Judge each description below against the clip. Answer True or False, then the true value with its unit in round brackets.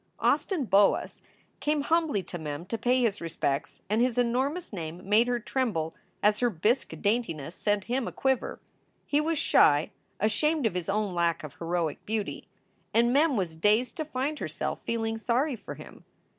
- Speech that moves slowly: False (170 wpm)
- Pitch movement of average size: False (6.2 semitones)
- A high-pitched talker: True (225 Hz)